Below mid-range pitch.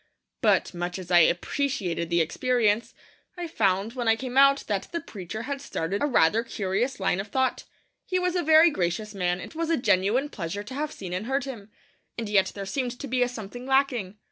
No: high, 225 Hz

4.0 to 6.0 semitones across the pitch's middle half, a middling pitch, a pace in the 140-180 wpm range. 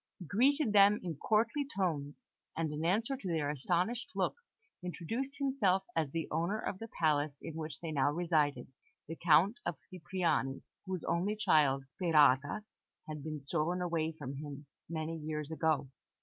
Yes: average, 4.8 semitones; medium, 165 Hz; average, 155 wpm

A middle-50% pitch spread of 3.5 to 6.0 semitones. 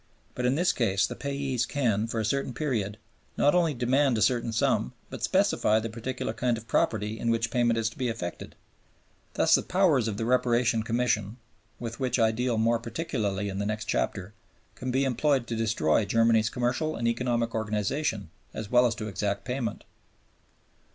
No: narrow, 2.5 semitones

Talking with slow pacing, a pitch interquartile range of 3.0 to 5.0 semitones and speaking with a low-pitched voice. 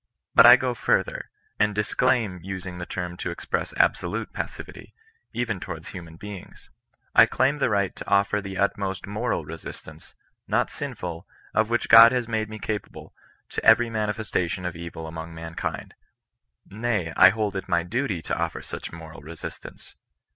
No: average, 160 wpm; average, 4.6 semitones; low, 100 Hz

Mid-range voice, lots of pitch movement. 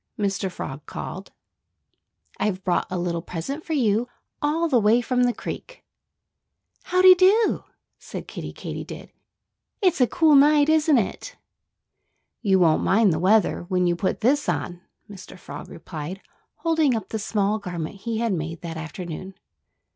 No: high, 210 Hz; wide, 8.1 semitones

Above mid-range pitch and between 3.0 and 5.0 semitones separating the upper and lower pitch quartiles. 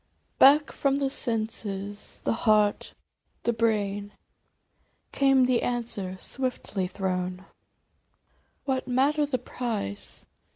Yes: high, 230 Hz; average, 4.6 semitones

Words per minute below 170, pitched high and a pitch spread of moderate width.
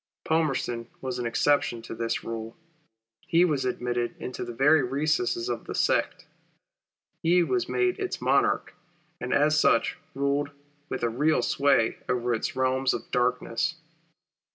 No: average, 145 wpm; low, 135 Hz; average, 4.2 semitones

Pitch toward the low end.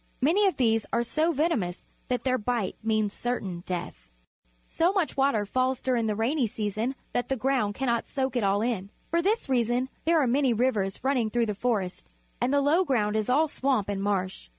No: high, 240 Hz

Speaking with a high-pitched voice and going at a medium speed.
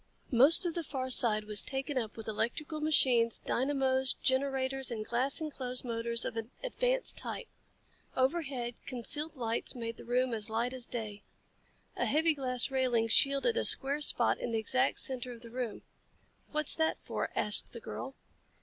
Yes: very high, 255 Hz; average, 170 wpm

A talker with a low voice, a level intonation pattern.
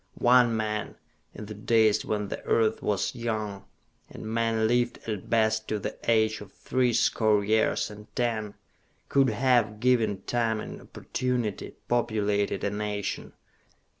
Yes: low, 110 Hz; narrow, 2.0 semitones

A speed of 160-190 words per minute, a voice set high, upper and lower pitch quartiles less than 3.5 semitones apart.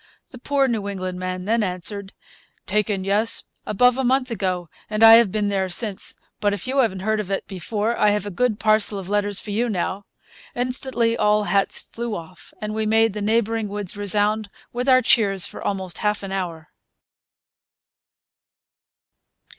Yes: average, 175 wpm; high, 210 Hz; narrow, 2.6 semitones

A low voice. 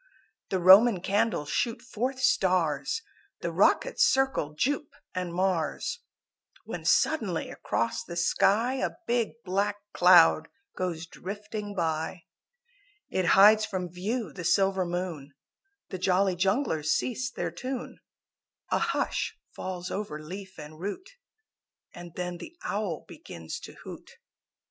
No: medium, 185 Hz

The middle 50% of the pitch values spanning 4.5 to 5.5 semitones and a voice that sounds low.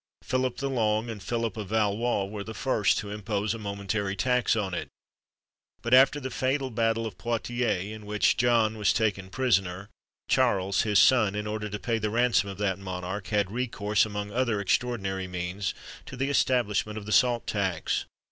No: average, 3.0 semitones; low, 105 Hz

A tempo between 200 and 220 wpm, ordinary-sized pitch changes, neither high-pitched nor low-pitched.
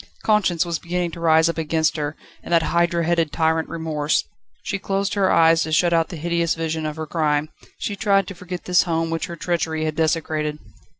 No: fast, 205 wpm; narrow, 1.5 semitones; medium, 165 Hz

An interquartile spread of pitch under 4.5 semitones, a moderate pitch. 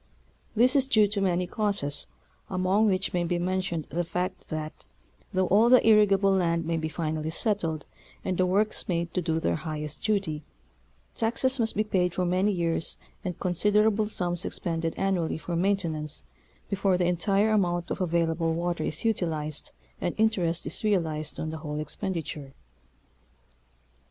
Yes: average, 3.6 semitones; medium, 180 Hz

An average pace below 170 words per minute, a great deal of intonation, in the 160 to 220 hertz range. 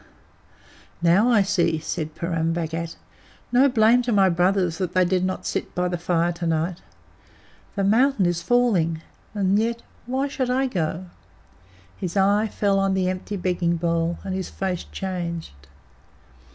No: average, 155 wpm; average, 3.4 semitones; medium, 185 Hz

